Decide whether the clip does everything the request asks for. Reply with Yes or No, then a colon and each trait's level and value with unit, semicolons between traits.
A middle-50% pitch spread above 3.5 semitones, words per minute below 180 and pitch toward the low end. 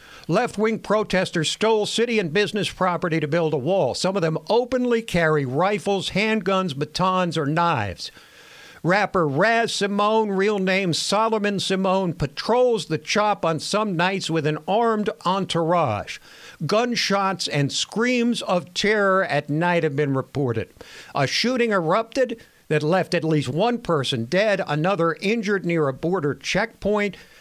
No: average, 4.7 semitones; average, 140 wpm; medium, 185 Hz